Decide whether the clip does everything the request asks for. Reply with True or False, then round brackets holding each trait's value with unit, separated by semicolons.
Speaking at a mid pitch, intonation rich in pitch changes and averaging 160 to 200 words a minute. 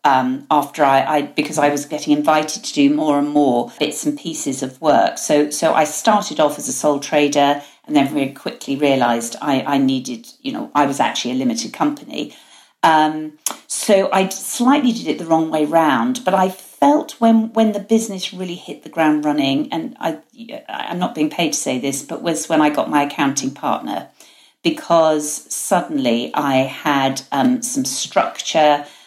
True (155 Hz; 6.1 semitones; 185 wpm)